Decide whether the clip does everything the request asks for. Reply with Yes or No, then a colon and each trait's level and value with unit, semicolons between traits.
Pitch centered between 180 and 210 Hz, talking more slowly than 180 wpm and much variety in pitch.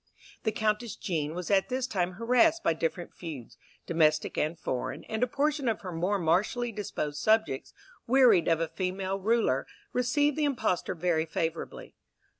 Yes: high, 190 Hz; average, 155 wpm; wide, 6.4 semitones